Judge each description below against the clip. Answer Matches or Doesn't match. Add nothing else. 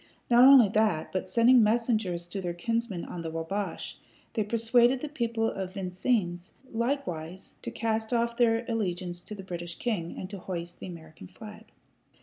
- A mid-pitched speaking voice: Doesn't match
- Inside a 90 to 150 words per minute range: Doesn't match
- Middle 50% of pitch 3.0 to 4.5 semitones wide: Doesn't match